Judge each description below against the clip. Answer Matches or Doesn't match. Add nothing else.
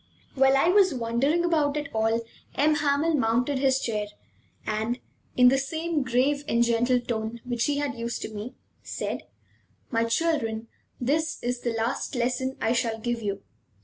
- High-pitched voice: Matches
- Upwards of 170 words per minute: Doesn't match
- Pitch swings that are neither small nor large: Matches